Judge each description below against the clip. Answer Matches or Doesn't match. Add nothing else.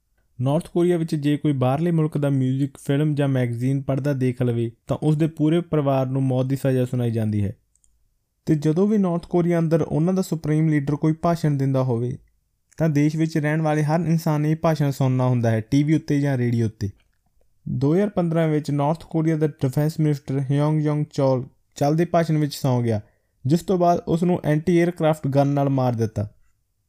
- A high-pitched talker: Doesn't match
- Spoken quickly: Matches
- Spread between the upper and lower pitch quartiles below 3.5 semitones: Doesn't match